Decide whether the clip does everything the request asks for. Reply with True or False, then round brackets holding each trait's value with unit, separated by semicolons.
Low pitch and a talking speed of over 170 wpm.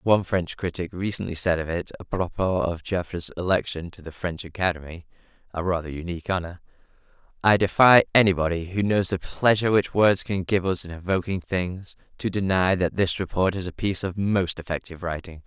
True (90 Hz; 180 wpm)